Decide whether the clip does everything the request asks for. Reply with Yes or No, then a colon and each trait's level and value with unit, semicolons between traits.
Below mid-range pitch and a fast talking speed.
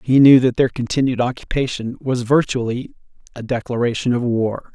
No: low, 125 Hz; average, 150 wpm